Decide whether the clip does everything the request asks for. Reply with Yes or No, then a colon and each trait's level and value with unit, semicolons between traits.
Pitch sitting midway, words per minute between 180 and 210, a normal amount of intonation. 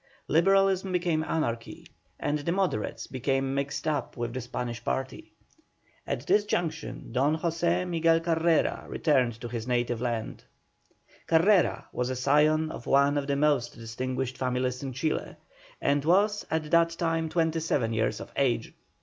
No: medium, 145 Hz; average, 150 wpm; average, 4.7 semitones